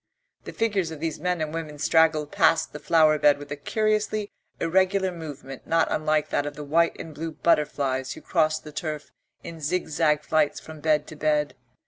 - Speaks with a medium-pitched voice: Yes, medium, 155 Hz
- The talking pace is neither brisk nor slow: Yes, average, 190 wpm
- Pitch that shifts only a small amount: Yes, narrow, 2.1 semitones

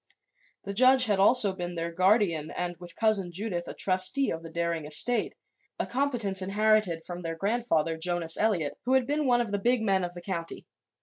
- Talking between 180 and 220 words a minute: Yes, average, 195 wpm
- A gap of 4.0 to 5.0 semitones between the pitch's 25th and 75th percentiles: Yes, average, 4.7 semitones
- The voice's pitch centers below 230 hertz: Yes, high, 190 Hz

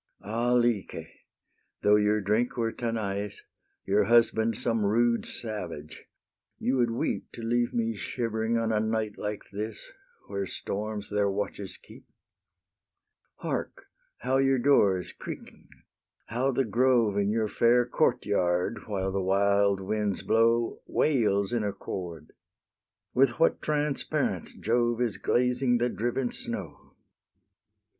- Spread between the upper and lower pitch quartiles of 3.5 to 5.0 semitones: No, average, 2.9 semitones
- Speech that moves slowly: Yes, slow, 130 wpm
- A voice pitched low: Yes, low, 110 Hz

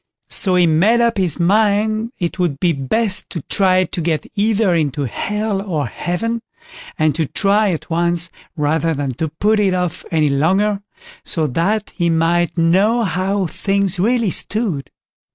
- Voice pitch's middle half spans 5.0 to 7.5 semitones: No, average, 4.3 semitones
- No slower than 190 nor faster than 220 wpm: No, average, 160 wpm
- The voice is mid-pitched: Yes, medium, 180 Hz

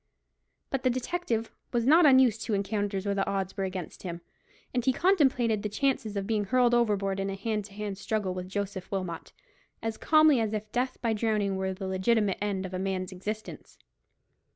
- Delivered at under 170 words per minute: No, average, 195 wpm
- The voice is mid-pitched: No, high, 210 Hz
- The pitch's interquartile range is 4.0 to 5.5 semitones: No, average, 3.5 semitones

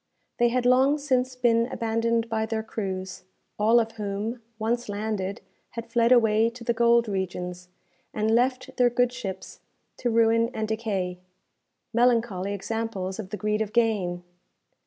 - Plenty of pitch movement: No, narrow, 2.6 semitones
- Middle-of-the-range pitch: No, high, 225 Hz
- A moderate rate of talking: Yes, average, 150 wpm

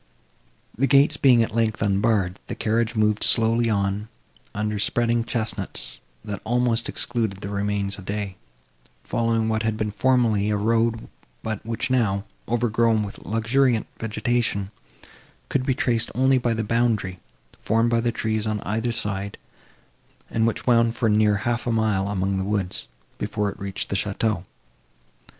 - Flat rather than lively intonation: Yes, narrow, 2.3 semitones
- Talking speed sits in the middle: Yes, average, 150 wpm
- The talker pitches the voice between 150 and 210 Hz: No, low, 110 Hz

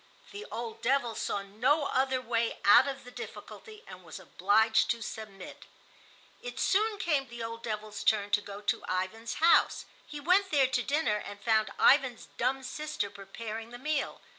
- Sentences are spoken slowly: No, average, 170 wpm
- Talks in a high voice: Yes, high, 240 Hz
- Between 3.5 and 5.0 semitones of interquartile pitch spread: Yes, average, 4.4 semitones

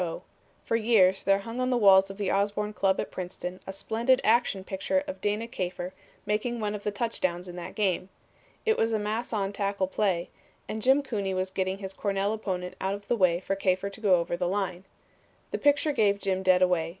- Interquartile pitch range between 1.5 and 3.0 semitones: Yes, average, 2.7 semitones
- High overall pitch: Yes, high, 200 Hz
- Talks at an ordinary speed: No, fast, 210 wpm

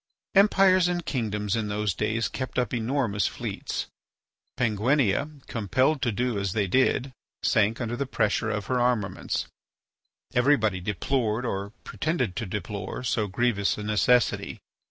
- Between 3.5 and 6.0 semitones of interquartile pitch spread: Yes, average, 3.8 semitones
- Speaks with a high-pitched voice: No, low, 115 Hz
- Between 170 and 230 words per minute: No, slow, 135 wpm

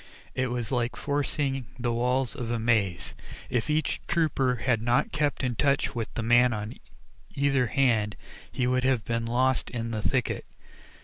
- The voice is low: Yes, low, 125 Hz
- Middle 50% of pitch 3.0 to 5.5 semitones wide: No, narrow, 2.5 semitones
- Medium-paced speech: Yes, average, 170 wpm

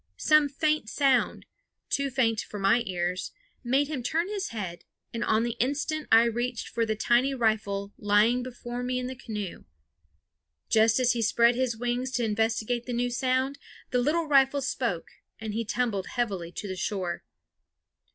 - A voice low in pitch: No, high, 240 Hz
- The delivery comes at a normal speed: Yes, average, 170 wpm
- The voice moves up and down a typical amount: Yes, average, 3.1 semitones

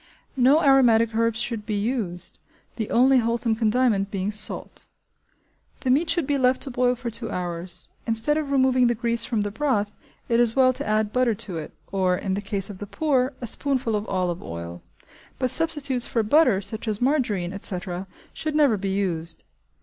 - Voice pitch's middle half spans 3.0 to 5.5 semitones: Yes, average, 4.4 semitones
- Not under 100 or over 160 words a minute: No, average, 190 wpm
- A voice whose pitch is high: Yes, high, 225 Hz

